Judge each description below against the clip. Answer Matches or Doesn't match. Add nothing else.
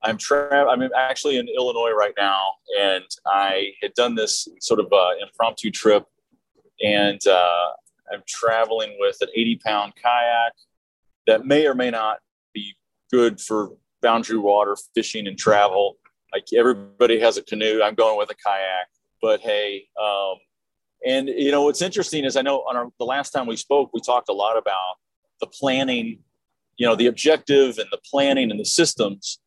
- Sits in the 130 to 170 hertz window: Doesn't match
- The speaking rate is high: Doesn't match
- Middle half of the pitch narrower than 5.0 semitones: Doesn't match